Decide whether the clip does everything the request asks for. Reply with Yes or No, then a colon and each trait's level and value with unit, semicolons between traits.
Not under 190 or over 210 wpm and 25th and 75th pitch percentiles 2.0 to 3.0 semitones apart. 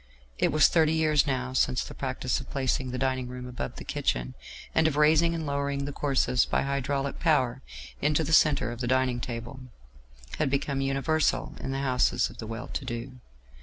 Yes: average, 195 wpm; narrow, 2.6 semitones